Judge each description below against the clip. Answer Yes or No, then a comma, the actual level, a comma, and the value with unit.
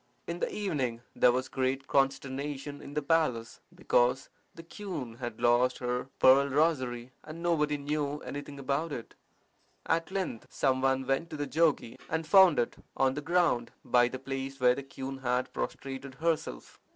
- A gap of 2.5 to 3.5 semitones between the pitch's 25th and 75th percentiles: Yes, average, 3.1 semitones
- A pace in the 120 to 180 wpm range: Yes, average, 165 wpm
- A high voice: No, low, 135 Hz